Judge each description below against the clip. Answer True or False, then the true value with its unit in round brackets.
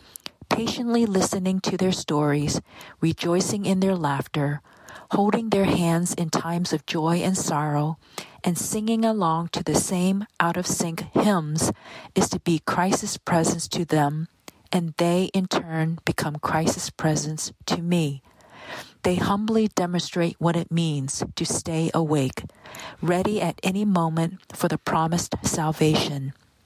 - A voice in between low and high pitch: True (170 Hz)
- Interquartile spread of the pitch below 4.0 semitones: True (3.0 semitones)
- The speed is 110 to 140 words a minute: True (135 wpm)